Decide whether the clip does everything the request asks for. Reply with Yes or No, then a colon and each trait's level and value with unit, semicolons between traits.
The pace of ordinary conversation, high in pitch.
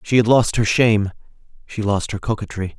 No: average, 195 wpm; low, 105 Hz